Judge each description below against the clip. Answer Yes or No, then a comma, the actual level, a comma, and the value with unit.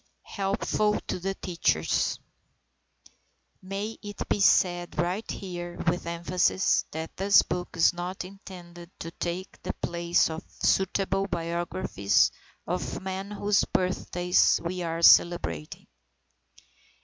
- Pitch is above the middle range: No, medium, 180 Hz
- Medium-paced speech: No, slow, 115 wpm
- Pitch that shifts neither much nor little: No, narrow, 2.1 semitones